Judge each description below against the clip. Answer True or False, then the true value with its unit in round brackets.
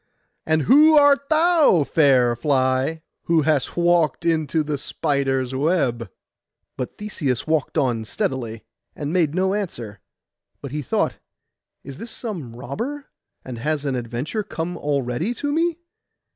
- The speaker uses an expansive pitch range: True (6.2 semitones)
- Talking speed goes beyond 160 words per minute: False (135 wpm)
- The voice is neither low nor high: True (150 Hz)